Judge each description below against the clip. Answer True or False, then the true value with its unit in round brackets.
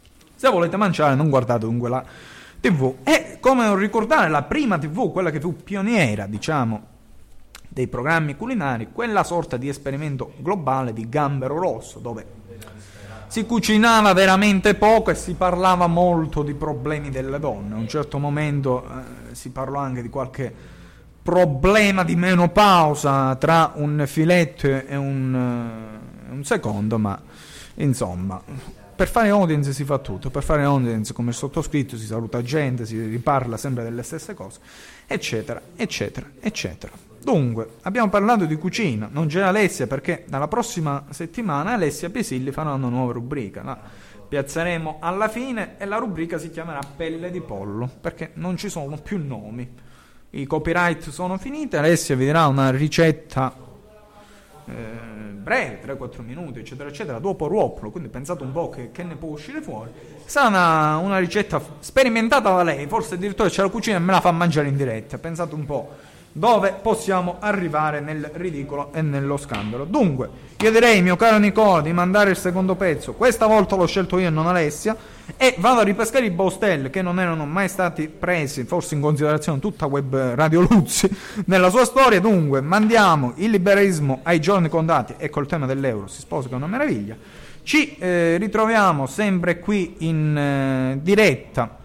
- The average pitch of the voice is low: False (160 Hz)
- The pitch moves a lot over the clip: True (6.2 semitones)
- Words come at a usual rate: True (160 wpm)